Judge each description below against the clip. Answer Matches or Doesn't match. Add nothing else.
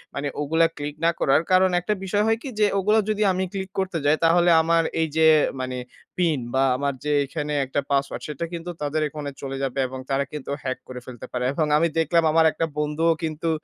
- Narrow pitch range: Doesn't match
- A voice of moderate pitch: Matches